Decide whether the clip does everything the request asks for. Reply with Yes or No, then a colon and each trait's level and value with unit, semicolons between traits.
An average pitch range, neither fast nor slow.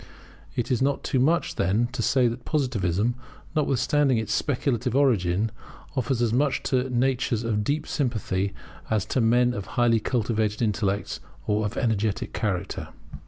Yes: average, 3.6 semitones; average, 150 wpm